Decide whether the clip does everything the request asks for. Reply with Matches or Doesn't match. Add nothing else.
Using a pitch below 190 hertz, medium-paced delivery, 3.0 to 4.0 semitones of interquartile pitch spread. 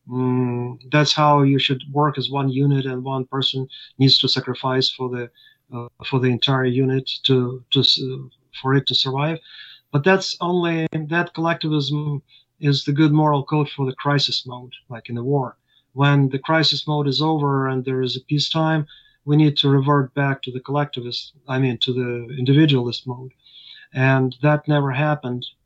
Doesn't match